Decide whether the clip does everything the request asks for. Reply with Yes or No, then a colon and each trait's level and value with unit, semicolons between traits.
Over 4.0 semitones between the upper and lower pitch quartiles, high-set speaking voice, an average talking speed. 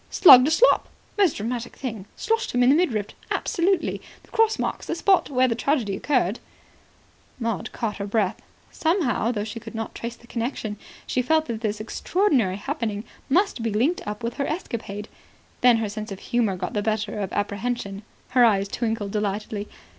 Yes: average, 4.5 semitones; high, 230 Hz; average, 180 wpm